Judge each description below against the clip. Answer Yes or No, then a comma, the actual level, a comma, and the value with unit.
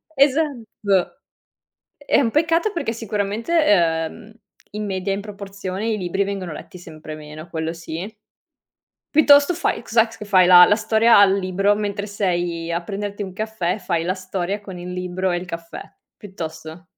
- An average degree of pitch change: Yes, average, 3.6 semitones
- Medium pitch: No, high, 195 Hz